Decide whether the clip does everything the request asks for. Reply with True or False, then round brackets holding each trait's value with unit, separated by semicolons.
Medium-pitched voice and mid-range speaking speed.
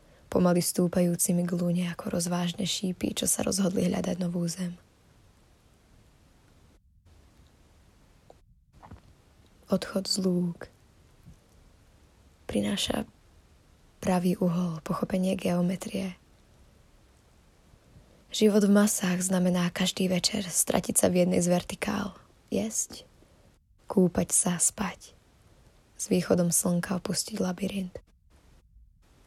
False (175 Hz; 85 wpm)